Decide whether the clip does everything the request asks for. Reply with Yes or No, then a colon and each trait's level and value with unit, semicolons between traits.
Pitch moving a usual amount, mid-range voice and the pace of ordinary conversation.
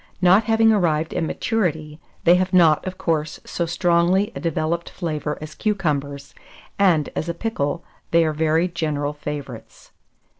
Yes: average, 3.1 semitones; medium, 165 Hz; average, 150 wpm